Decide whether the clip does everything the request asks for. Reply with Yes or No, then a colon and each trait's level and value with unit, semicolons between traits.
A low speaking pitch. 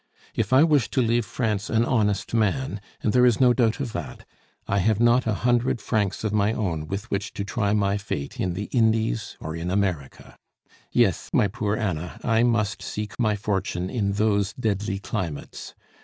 Yes: low, 105 Hz